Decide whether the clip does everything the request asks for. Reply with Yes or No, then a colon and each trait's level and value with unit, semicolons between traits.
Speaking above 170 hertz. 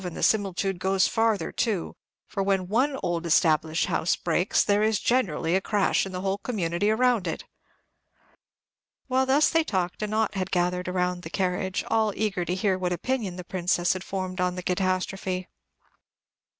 Yes: high, 190 Hz